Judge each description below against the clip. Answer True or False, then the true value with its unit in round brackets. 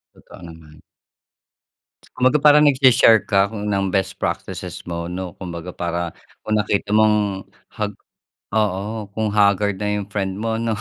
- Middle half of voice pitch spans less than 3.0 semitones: True (2.5 semitones)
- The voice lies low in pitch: True (100 Hz)